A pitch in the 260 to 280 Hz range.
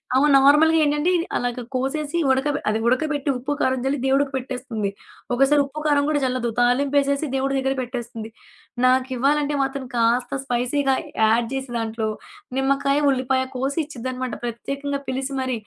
Yes: very high, 265 Hz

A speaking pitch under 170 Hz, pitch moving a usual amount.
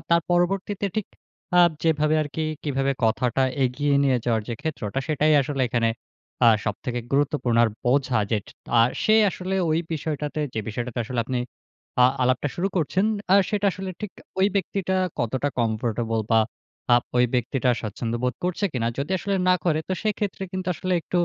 No: medium, 140 Hz; wide, 6.5 semitones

